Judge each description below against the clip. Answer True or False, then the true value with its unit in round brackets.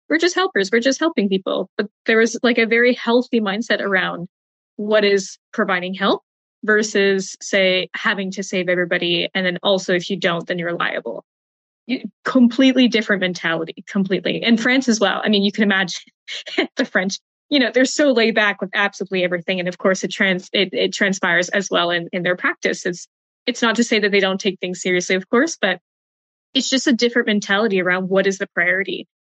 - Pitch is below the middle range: False (200 Hz)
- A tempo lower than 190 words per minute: False (200 wpm)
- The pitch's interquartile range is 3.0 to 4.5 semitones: True (3.8 semitones)